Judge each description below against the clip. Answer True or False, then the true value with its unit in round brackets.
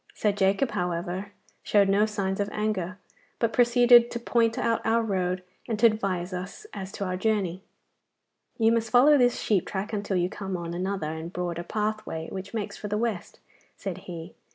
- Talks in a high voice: True (200 Hz)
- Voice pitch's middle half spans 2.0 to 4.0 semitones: True (3.5 semitones)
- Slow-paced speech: False (180 wpm)